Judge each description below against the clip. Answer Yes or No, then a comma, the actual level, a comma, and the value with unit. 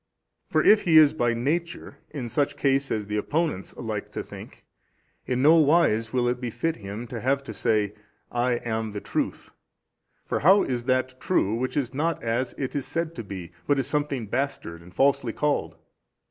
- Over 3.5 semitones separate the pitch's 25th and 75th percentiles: Yes, average, 4.3 semitones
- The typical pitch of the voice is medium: No, low, 130 Hz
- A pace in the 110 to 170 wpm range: No, average, 190 wpm